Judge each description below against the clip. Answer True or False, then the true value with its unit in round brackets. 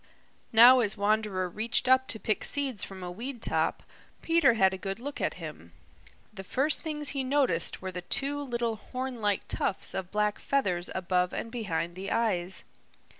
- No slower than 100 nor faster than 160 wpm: False (175 wpm)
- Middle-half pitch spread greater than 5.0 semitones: True (5.4 semitones)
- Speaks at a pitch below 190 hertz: False (220 Hz)